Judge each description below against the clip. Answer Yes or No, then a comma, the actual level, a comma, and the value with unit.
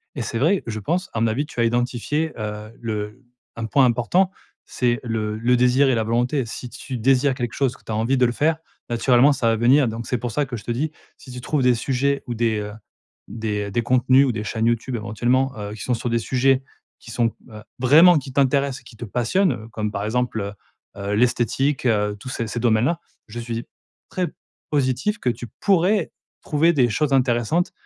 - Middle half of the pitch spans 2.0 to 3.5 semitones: Yes, average, 3.1 semitones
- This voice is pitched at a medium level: No, low, 120 Hz